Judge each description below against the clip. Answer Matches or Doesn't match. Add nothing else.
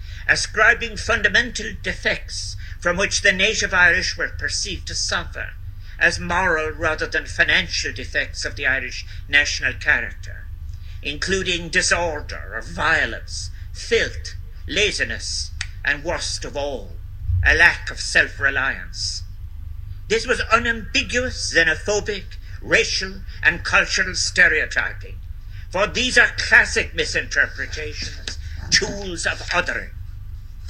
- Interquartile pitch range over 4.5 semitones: Doesn't match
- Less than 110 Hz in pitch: Matches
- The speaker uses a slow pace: Matches